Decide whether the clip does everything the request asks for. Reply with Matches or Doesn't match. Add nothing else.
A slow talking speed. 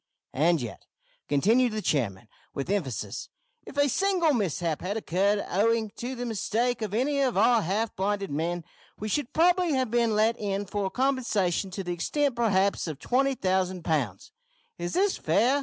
Doesn't match